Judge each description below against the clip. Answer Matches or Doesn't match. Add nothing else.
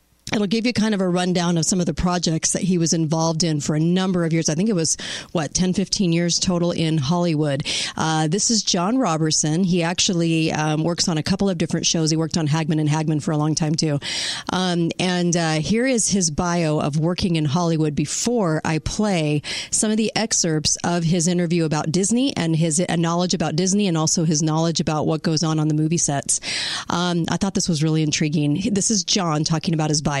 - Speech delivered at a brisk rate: Matches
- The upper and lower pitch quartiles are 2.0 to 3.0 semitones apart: Matches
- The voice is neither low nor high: Matches